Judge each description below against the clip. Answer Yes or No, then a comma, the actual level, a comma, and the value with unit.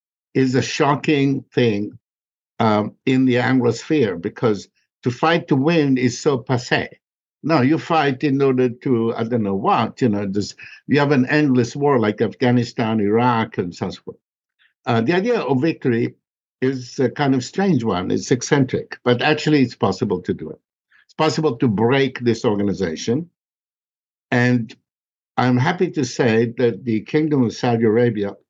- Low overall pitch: Yes, low, 125 Hz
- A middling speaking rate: No, fast, 160 wpm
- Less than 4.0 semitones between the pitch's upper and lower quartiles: Yes, average, 3.6 semitones